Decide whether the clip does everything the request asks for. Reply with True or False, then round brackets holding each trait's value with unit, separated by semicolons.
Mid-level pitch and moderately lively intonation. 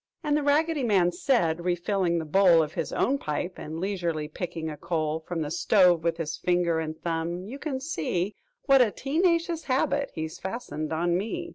False (175 Hz; 8.1 semitones)